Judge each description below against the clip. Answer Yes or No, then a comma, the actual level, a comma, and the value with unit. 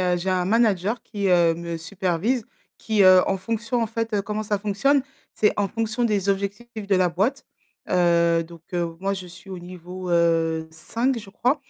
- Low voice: No, high, 195 Hz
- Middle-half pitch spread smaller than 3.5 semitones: No, average, 3.9 semitones